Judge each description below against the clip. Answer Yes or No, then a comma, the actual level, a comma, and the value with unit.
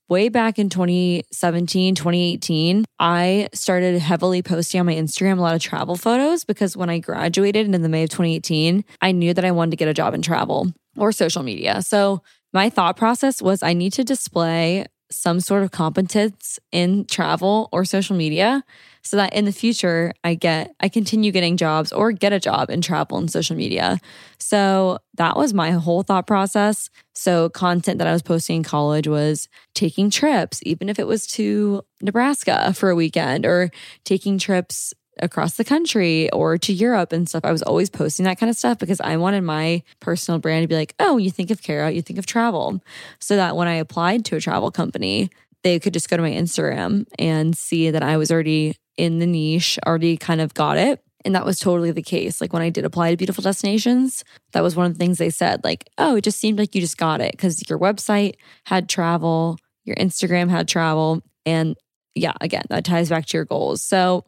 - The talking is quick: Yes, fast, 210 wpm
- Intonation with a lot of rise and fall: No, average, 3.3 semitones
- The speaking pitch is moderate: Yes, medium, 180 Hz